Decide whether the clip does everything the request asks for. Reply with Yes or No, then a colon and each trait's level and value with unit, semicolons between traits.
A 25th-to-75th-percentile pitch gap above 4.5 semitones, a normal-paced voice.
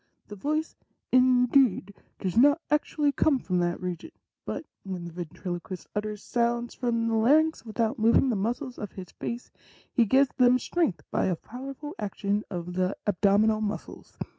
Yes: average, 4.9 semitones; average, 170 wpm